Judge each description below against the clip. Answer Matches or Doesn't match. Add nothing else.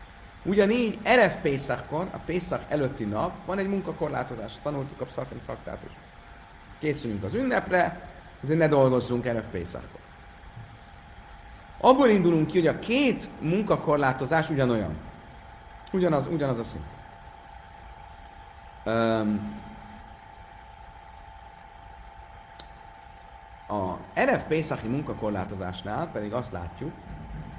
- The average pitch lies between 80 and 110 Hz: Doesn't match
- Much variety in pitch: Matches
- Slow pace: Matches